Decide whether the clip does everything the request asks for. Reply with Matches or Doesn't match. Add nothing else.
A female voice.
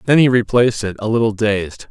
Doesn't match